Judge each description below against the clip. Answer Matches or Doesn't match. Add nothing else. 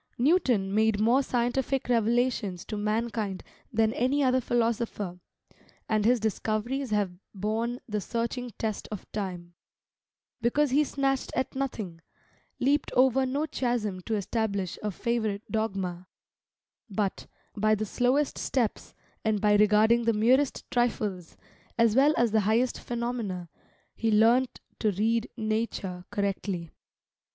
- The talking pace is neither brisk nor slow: Doesn't match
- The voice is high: Matches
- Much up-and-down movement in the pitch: Doesn't match